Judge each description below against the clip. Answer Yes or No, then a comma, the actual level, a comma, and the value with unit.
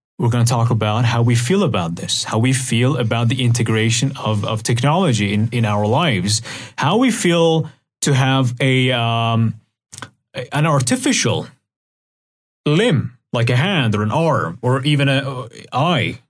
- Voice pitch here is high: No, low, 125 Hz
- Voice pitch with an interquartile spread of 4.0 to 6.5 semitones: No, average, 3.4 semitones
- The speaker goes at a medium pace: No, fast, 160 wpm